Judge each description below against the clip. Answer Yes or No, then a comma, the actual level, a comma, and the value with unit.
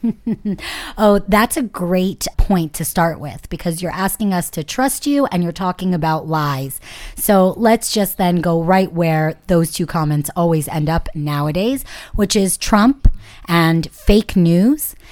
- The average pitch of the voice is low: No, medium, 180 Hz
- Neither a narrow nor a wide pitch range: Yes, average, 4.2 semitones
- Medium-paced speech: Yes, average, 160 wpm